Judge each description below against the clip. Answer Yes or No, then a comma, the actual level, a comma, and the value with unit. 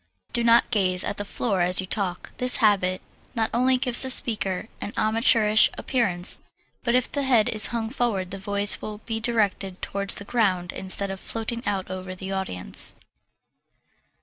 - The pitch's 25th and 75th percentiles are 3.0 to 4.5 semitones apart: Yes, average, 3.6 semitones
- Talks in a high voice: Yes, high, 205 Hz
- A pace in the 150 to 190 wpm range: Yes, average, 175 wpm